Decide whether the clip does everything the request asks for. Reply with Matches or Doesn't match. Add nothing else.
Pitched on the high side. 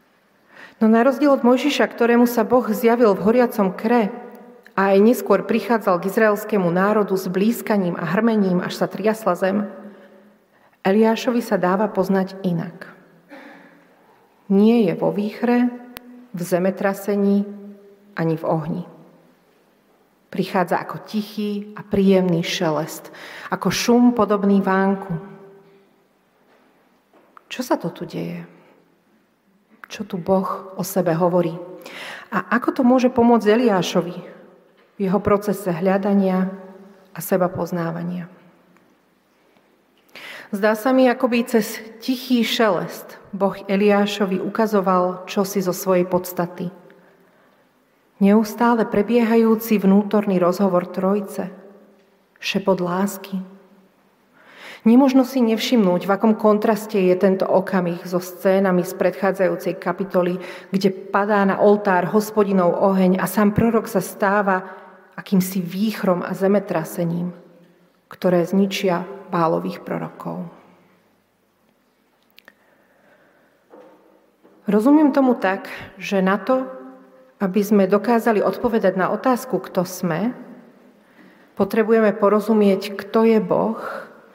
Matches